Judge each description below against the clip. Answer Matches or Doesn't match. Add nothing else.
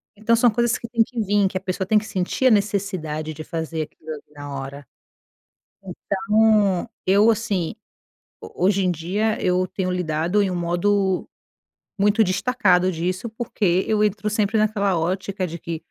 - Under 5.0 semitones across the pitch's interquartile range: Matches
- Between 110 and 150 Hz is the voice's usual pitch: Doesn't match